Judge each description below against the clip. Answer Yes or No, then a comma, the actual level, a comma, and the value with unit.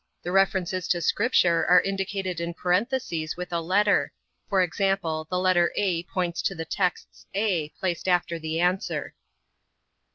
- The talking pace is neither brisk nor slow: Yes, average, 150 wpm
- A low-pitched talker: No, medium, 180 Hz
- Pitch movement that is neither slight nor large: No, narrow, 2.2 semitones